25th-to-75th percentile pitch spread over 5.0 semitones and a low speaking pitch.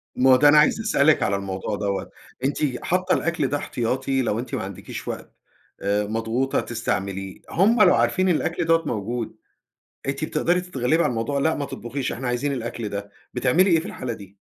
Yes: wide, 5.4 semitones; low, 130 Hz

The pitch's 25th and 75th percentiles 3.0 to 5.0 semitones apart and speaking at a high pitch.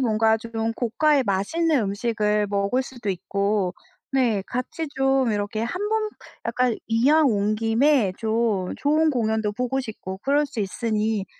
Yes: average, 4.3 semitones; high, 225 Hz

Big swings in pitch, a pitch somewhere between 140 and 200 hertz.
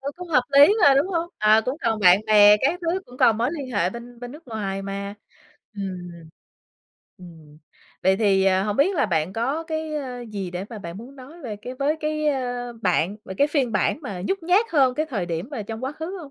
No: wide, 7.0 semitones; high, 235 Hz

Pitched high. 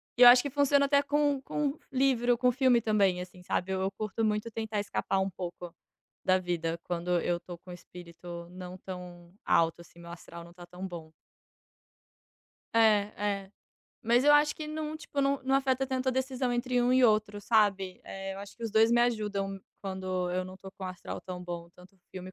Yes: high, 200 Hz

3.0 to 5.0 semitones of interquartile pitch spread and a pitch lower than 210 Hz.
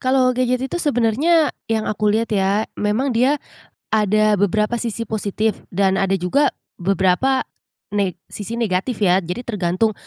No: average, 3.9 semitones; high, 215 Hz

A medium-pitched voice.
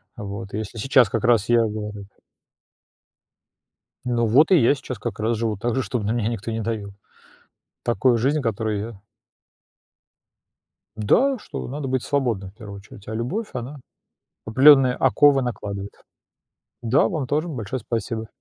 No: low, 115 Hz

